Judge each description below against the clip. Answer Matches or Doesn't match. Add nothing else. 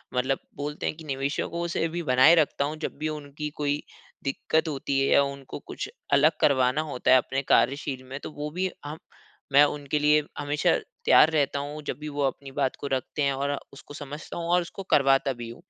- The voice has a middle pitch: Matches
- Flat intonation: Matches